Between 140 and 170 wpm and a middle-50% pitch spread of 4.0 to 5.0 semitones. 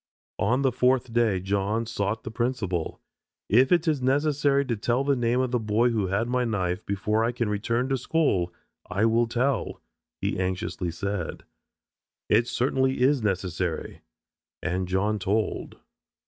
Yes: average, 155 wpm; average, 4.4 semitones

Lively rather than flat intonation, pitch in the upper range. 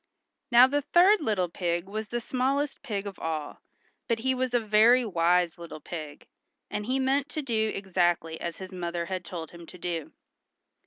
Yes: wide, 6.7 semitones; high, 200 Hz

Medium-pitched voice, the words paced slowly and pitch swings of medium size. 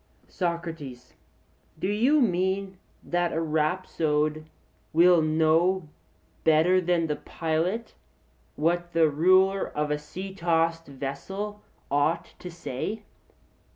Yes: medium, 170 Hz; slow, 105 wpm; average, 3.1 semitones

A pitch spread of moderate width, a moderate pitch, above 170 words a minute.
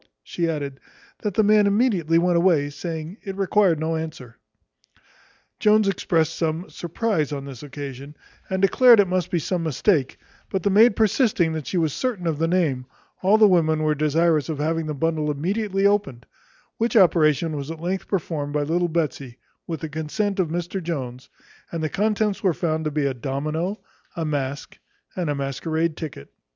Yes: average, 4.1 semitones; medium, 165 Hz; average, 180 wpm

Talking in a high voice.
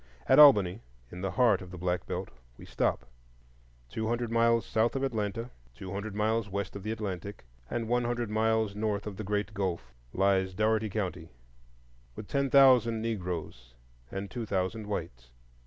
No: low, 105 Hz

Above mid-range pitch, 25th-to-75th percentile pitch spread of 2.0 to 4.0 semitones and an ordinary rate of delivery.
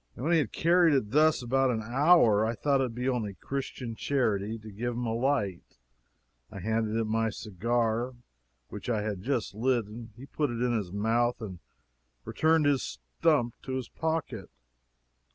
No: low, 120 Hz; average, 3.7 semitones; average, 180 wpm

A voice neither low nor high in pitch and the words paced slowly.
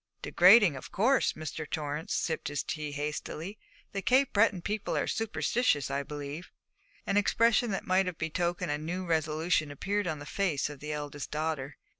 No: medium, 160 Hz; average, 175 wpm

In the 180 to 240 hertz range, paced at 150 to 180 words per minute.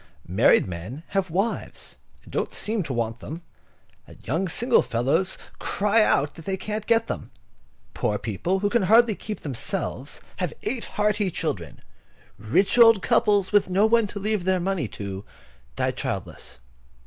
Yes: high, 190 Hz; average, 160 wpm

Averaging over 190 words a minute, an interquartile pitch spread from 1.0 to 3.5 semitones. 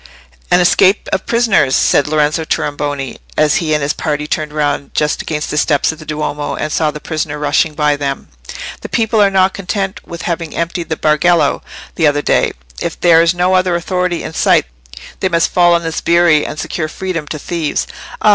Yes: average, 200 wpm; average, 2.9 semitones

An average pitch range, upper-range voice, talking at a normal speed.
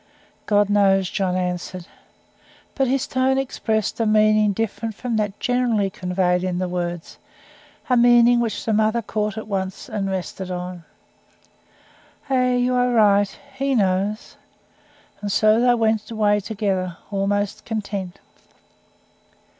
No: average, 3.3 semitones; high, 210 Hz; slow, 130 wpm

